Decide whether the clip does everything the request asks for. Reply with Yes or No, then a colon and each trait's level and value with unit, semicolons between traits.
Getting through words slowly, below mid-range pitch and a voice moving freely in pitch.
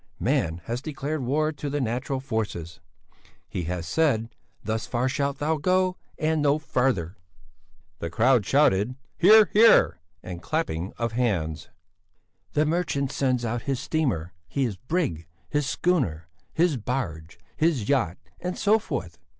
Yes: slow, 130 wpm; low, 130 Hz; wide, 7.7 semitones